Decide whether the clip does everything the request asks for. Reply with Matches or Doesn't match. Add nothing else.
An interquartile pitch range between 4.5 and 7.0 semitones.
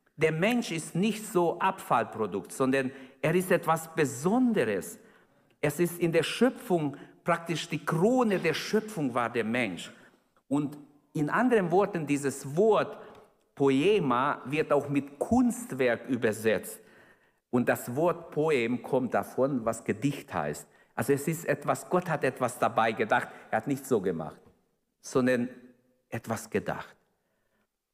Matches